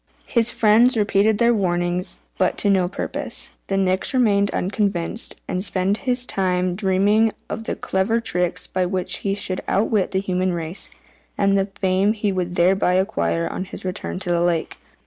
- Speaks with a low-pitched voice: No, high, 190 Hz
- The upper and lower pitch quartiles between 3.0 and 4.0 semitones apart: No, narrow, 2.4 semitones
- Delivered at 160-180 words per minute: Yes, average, 175 wpm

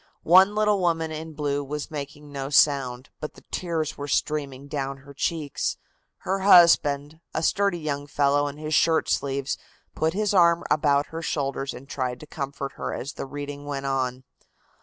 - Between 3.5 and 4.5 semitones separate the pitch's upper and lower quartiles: No, average, 2.7 semitones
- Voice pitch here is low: No, medium, 145 Hz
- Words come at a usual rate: Yes, average, 175 wpm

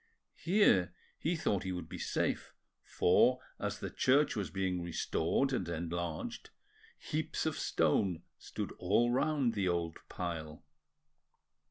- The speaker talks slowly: Yes, slow, 130 wpm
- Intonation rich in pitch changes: Yes, wide, 6.4 semitones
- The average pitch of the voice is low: Yes, very low, 90 Hz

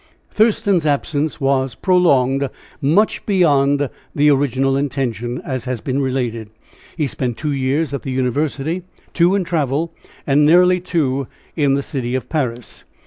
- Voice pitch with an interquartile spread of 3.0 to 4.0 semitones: Yes, average, 3.4 semitones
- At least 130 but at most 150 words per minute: Yes, average, 140 wpm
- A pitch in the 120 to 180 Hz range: Yes, medium, 140 Hz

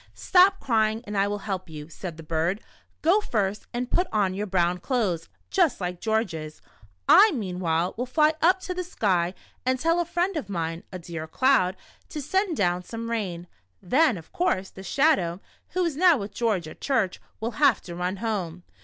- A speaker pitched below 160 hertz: No, high, 205 Hz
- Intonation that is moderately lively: No, wide, 7.9 semitones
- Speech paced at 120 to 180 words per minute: No, average, 190 wpm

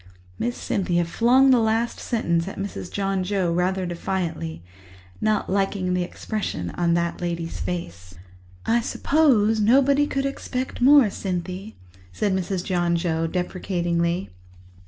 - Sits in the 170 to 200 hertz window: Yes, high, 190 Hz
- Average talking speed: No, slow, 130 wpm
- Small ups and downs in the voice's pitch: No, average, 4.4 semitones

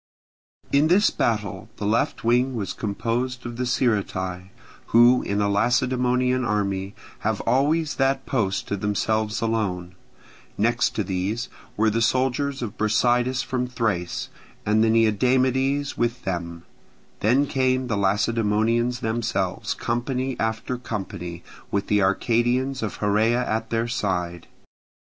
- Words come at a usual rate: No, slow, 130 wpm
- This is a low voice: Yes, low, 115 Hz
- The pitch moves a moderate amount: Yes, average, 3.6 semitones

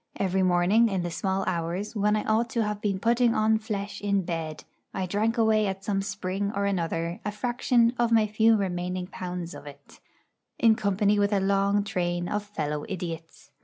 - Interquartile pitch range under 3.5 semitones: Yes, average, 3.0 semitones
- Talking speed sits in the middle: Yes, average, 190 wpm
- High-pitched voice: Yes, high, 200 Hz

